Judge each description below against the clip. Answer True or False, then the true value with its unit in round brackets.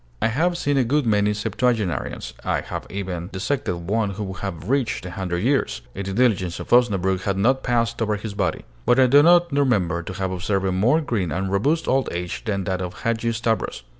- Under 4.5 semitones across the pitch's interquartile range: False (4.8 semitones)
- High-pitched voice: False (105 Hz)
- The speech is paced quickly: True (215 wpm)